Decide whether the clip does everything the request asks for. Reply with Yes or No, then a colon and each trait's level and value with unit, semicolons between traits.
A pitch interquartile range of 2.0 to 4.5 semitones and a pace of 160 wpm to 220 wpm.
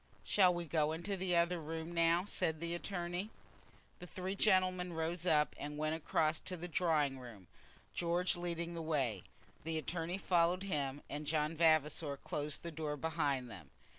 Yes: average, 2.7 semitones; average, 170 wpm